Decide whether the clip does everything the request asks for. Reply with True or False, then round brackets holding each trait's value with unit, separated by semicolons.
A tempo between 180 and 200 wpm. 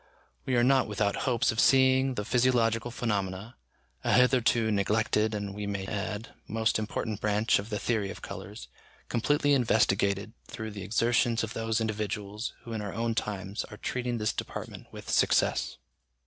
False (160 wpm)